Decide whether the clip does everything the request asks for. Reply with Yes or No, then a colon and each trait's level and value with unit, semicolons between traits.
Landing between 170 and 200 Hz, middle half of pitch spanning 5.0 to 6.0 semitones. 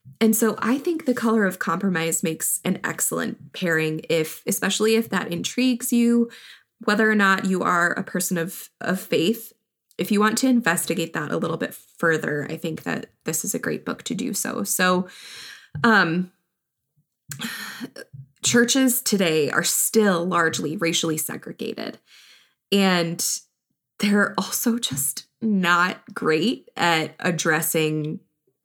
Yes: medium, 185 Hz; wide, 5.4 semitones